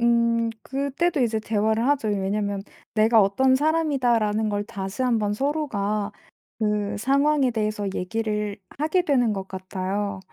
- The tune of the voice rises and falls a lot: No, average, 4.2 semitones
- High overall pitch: Yes, high, 220 Hz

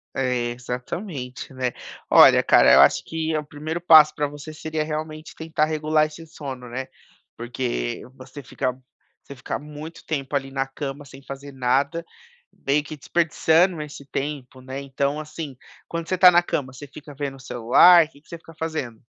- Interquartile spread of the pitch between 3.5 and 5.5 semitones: No, average, 3.0 semitones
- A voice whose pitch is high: No, medium, 145 Hz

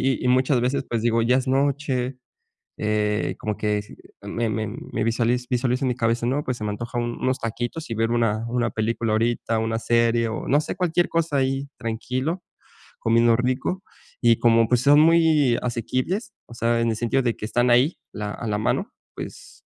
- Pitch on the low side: Yes, low, 120 Hz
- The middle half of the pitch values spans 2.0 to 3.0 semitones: Yes, narrow, 2.5 semitones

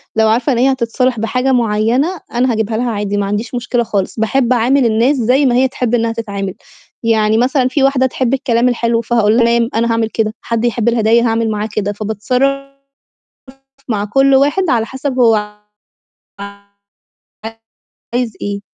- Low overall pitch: No, high, 235 Hz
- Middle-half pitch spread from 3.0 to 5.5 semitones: No, narrow, 2.6 semitones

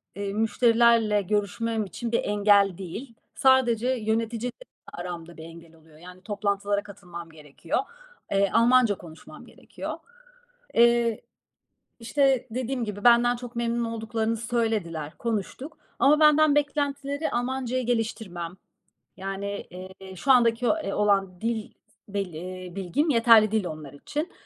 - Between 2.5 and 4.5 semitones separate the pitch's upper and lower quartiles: Yes, average, 4.0 semitones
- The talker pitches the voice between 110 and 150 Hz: No, high, 220 Hz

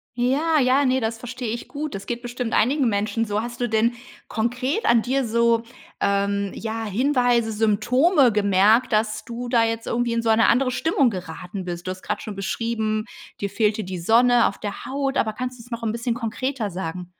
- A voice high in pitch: Yes, high, 230 Hz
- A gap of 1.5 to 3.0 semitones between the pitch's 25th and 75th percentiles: Yes, average, 2.7 semitones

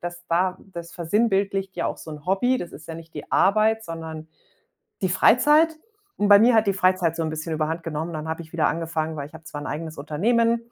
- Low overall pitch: No, medium, 170 Hz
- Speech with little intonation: No, average, 4.0 semitones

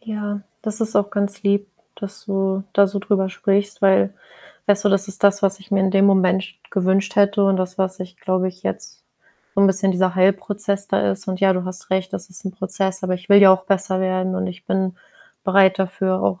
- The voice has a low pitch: No, high, 195 Hz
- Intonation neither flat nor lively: No, narrow, 1.3 semitones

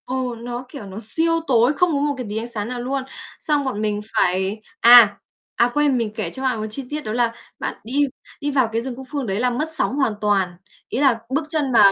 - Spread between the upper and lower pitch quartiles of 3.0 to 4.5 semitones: Yes, average, 4.2 semitones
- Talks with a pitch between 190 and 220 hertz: No, high, 245 Hz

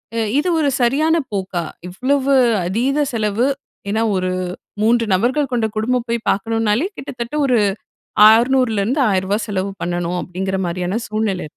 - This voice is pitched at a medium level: No, high, 225 Hz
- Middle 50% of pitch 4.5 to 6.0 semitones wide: Yes, average, 4.8 semitones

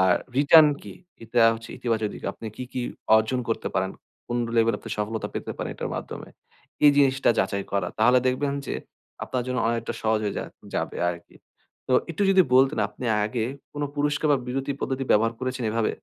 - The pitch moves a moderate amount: Yes, average, 3.3 semitones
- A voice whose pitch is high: No, low, 125 Hz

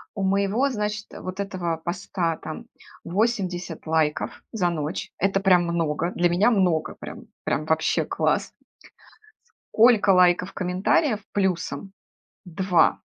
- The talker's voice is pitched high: No, medium, 180 Hz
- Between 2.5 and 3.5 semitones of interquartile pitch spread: Yes, average, 2.8 semitones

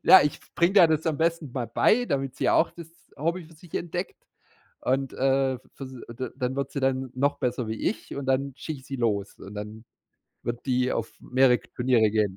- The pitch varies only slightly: No, average, 3.9 semitones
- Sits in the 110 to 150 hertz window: Yes, low, 135 Hz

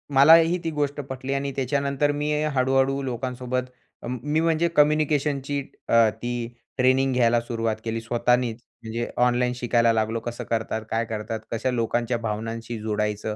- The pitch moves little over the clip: No, average, 3.3 semitones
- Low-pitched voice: Yes, low, 125 Hz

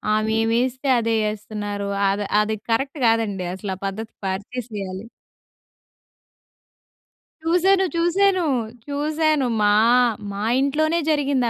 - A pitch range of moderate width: No, wide, 6.6 semitones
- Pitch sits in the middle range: No, high, 230 Hz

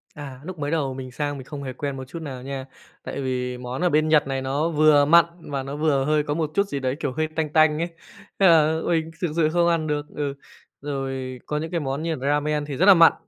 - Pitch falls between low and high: Yes, medium, 150 Hz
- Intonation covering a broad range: No, average, 2.9 semitones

